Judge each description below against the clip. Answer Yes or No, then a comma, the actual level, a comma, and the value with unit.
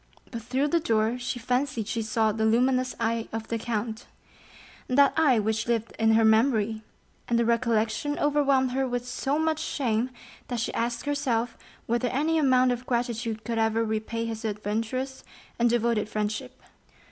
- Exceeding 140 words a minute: Yes, average, 160 wpm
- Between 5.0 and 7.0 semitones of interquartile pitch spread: No, narrow, 2.5 semitones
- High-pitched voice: Yes, high, 235 Hz